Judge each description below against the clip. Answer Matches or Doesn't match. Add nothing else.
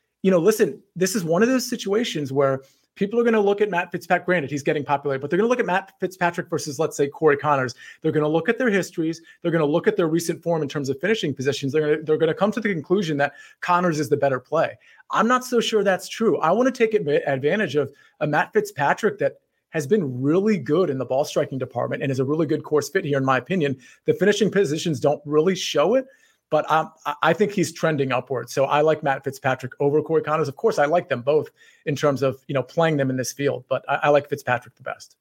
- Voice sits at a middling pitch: Matches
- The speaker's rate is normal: Doesn't match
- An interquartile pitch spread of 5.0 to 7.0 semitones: Matches